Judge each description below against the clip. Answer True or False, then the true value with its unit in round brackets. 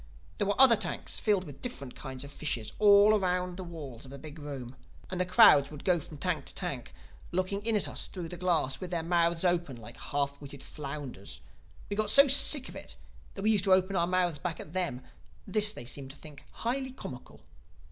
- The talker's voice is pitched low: False (175 Hz)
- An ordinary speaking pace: False (220 wpm)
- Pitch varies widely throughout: True (5.7 semitones)